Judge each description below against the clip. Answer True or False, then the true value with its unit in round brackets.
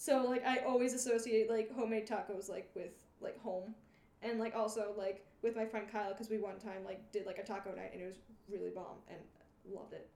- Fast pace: True (225 wpm)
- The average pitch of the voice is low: False (220 Hz)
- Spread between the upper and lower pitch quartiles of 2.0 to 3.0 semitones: True (2.7 semitones)